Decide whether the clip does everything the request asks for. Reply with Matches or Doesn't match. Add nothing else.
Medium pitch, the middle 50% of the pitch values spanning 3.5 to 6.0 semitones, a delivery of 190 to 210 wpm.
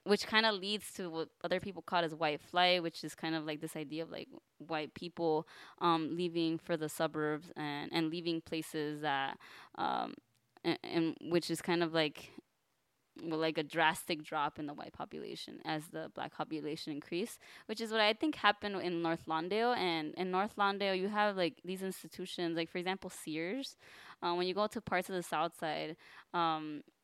Doesn't match